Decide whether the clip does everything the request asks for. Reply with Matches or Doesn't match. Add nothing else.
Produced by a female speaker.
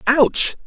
Doesn't match